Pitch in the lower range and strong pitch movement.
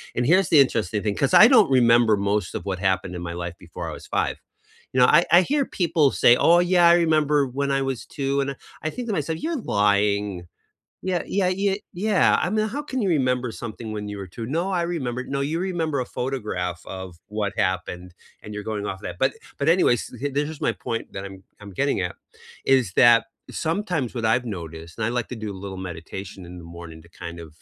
Yes: low, 125 Hz; wide, 8.5 semitones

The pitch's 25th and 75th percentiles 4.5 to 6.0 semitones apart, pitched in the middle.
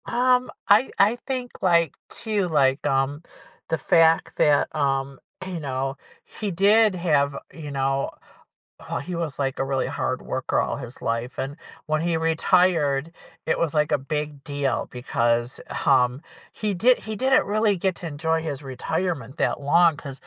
Yes: average, 5.0 semitones; medium, 155 Hz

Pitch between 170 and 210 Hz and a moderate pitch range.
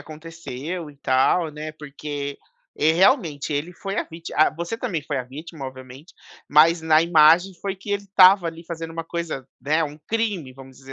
No: medium, 160 Hz; average, 3.2 semitones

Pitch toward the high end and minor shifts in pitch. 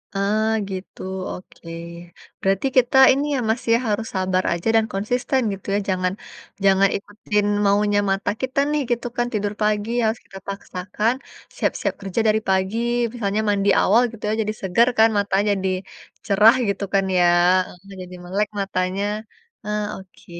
Yes: high, 205 Hz; narrow, 2.2 semitones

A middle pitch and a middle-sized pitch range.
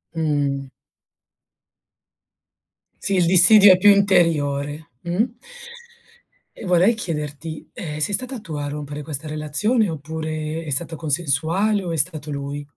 Yes: medium, 160 Hz; average, 3.8 semitones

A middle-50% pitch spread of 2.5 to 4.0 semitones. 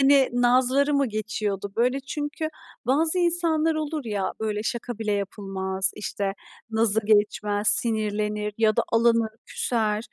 No: average, 4.5 semitones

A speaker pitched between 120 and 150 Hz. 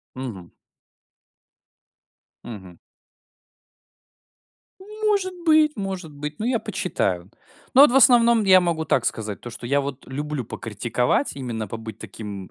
Yes: medium, 140 Hz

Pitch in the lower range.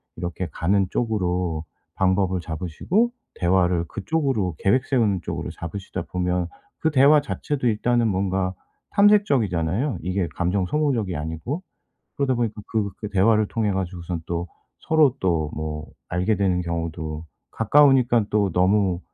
Yes: very low, 95 Hz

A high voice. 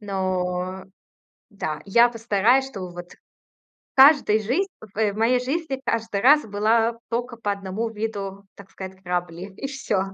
Yes: high, 210 Hz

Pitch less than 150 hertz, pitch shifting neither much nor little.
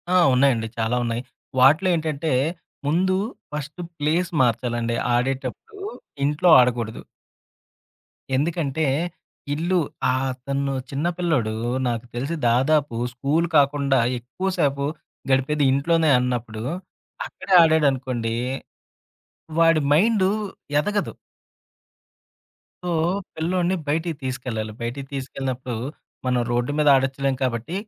Yes: medium, 140 Hz; average, 4.5 semitones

